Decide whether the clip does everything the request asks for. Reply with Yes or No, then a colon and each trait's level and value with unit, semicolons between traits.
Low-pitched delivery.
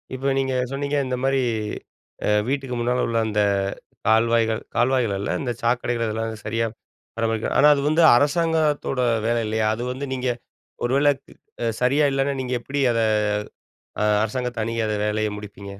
Yes: low, 120 Hz